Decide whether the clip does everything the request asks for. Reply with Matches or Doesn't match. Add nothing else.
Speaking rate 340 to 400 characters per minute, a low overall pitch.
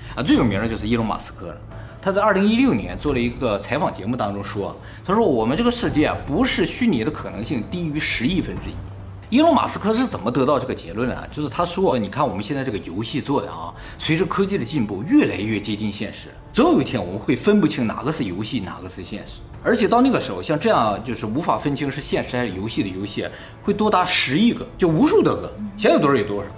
Matches